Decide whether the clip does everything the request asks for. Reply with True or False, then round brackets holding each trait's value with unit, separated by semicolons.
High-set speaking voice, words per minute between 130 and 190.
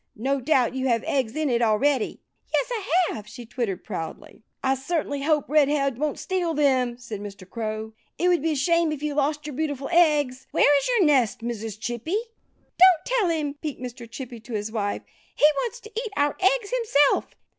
False (280 Hz; 200 wpm)